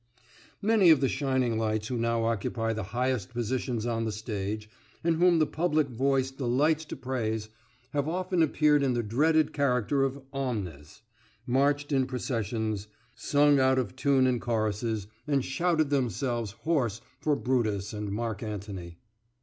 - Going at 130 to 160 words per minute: Yes, average, 150 wpm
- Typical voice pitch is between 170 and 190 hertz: No, low, 125 Hz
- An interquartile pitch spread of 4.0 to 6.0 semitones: Yes, average, 4.4 semitones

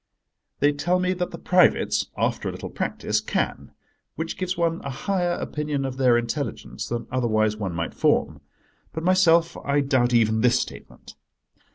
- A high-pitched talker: No, medium, 140 Hz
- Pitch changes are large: Yes, wide, 6.5 semitones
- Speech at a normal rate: Yes, average, 160 wpm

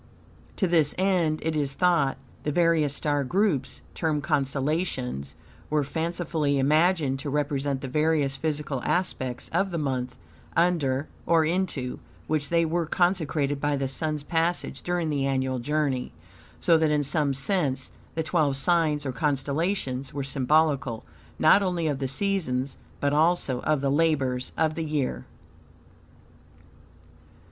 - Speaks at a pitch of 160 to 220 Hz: No, medium, 150 Hz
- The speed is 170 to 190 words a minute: No, average, 140 wpm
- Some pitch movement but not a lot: Yes, average, 3.4 semitones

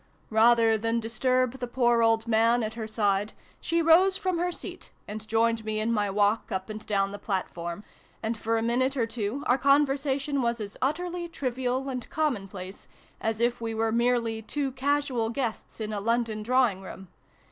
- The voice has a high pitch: Yes, high, 230 Hz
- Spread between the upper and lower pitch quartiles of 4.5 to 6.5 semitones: No, average, 3.3 semitones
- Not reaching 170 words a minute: No, average, 180 wpm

